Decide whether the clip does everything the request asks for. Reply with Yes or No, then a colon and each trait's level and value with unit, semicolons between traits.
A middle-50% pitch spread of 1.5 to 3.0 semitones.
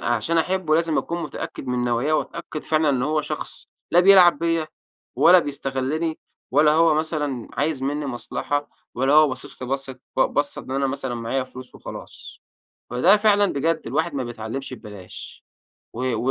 No: average, 3.8 semitones